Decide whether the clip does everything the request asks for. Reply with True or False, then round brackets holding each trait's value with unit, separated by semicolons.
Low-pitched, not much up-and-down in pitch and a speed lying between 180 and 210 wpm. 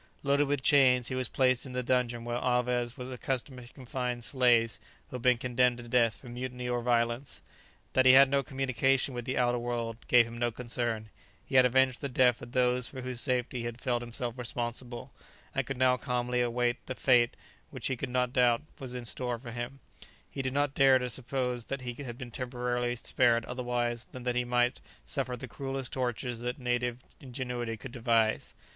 True (125 Hz; 1.2 semitones; 200 wpm)